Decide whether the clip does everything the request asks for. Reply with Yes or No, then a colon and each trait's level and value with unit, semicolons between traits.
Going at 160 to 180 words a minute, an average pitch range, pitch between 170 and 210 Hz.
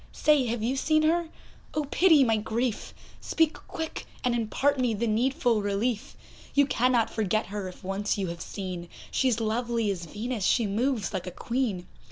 No: average, 175 wpm; average, 4.3 semitones; high, 230 Hz